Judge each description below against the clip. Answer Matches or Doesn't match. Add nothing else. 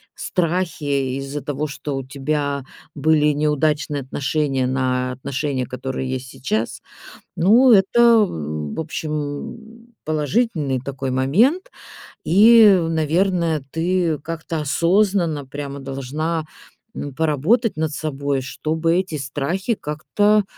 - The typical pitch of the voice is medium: Matches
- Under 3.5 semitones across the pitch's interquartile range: Doesn't match